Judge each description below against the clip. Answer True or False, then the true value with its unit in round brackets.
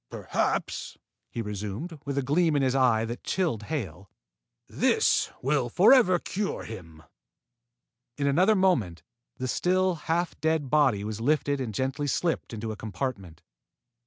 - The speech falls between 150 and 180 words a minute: False (140 wpm)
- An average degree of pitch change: False (6.7 semitones)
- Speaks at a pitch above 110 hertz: True (135 Hz)